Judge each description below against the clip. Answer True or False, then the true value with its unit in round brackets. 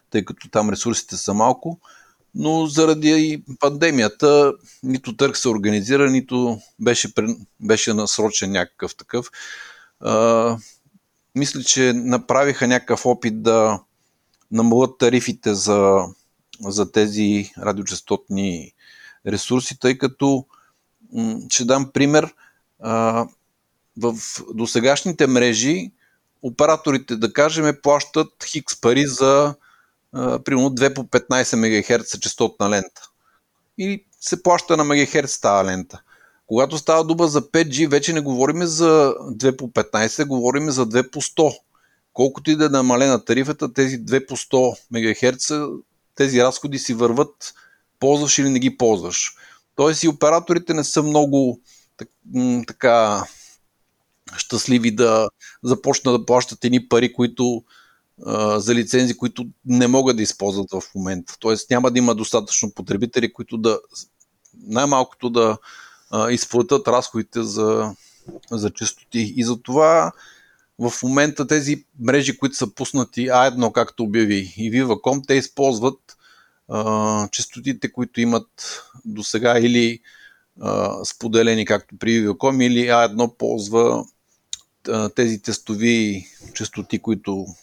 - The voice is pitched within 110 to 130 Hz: True (125 Hz)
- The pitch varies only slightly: False (3.8 semitones)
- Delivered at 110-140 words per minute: True (120 wpm)